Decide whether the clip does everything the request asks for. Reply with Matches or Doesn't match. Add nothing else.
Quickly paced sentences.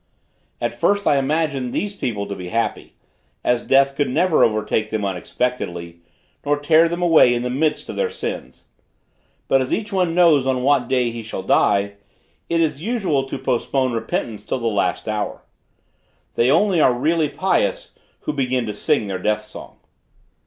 Doesn't match